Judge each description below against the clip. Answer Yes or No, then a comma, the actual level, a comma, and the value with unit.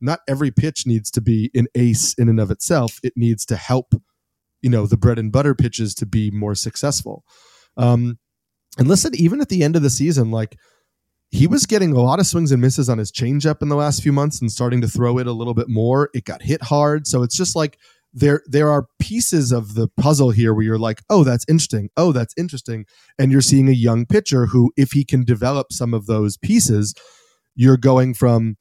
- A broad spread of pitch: No, average, 3.9 semitones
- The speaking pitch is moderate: No, low, 125 Hz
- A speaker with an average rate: No, fast, 225 wpm